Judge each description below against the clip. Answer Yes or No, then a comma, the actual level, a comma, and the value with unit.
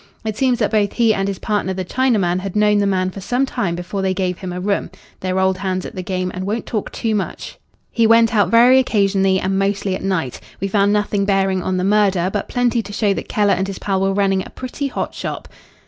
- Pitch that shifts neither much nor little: No, narrow, 2.0 semitones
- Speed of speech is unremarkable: No, fast, 245 wpm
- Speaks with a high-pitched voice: Yes, high, 195 Hz